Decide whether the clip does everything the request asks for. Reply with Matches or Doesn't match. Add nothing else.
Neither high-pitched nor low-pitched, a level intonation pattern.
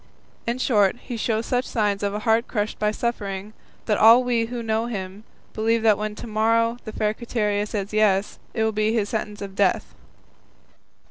Doesn't match